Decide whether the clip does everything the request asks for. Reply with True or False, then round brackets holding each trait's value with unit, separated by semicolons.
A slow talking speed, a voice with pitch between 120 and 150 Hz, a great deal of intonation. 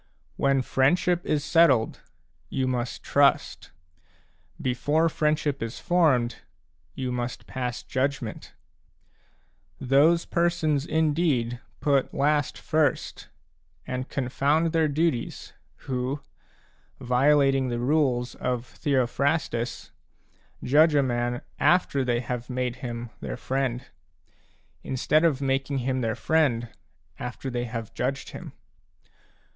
False (110 wpm; 135 Hz; 3.4 semitones)